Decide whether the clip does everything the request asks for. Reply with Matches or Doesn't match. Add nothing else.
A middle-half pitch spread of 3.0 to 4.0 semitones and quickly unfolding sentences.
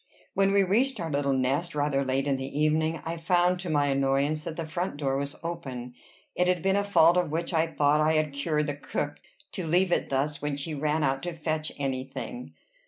Matches